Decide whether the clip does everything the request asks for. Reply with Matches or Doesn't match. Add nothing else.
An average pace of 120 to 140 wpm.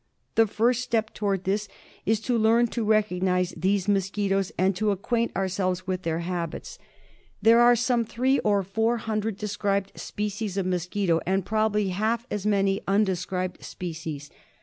Doesn't match